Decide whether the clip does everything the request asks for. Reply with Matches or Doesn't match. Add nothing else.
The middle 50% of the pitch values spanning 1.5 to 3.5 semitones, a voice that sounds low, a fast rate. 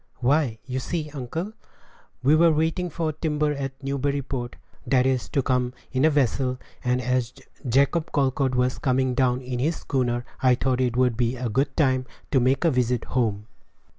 Doesn't match